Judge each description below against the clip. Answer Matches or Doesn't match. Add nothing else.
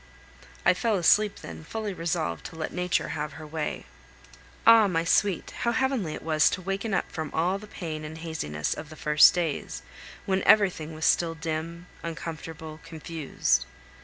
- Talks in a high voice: Doesn't match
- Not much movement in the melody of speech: Doesn't match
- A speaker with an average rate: Matches